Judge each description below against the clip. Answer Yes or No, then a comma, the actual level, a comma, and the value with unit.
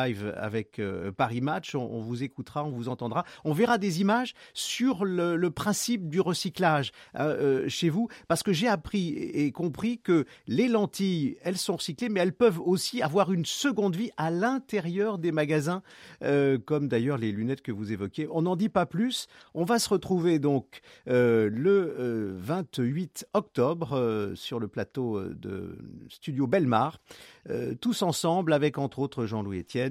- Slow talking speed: No, average, 165 wpm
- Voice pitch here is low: No, medium, 165 Hz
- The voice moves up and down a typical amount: No, wide, 7.5 semitones